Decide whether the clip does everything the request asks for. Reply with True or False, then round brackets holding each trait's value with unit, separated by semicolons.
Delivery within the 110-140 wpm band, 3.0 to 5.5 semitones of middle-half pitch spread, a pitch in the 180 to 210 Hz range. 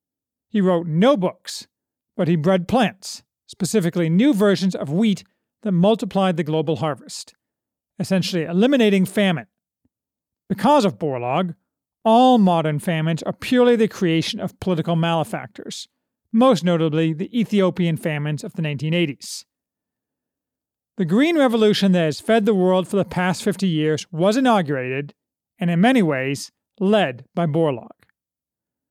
True (135 wpm; 4.6 semitones; 185 Hz)